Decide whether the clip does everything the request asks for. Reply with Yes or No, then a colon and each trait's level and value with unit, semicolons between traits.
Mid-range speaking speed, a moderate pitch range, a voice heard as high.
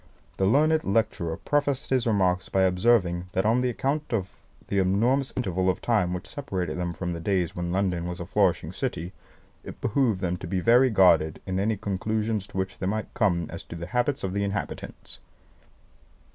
No: average, 185 wpm; average, 4.3 semitones; very low, 95 Hz